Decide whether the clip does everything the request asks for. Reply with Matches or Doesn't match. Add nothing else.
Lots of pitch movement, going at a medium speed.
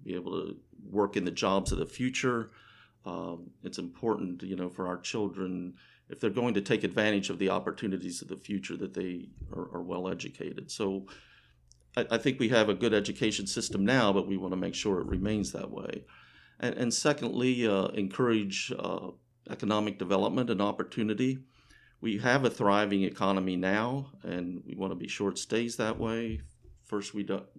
Doesn't match